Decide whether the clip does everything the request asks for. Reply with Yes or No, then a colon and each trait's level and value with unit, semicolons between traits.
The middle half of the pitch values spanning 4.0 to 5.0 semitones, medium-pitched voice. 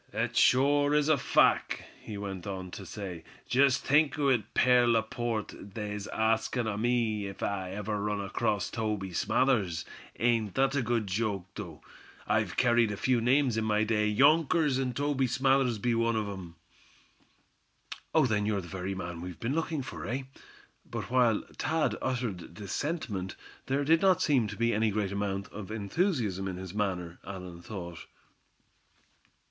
No: average, 4.6 semitones; low, 110 Hz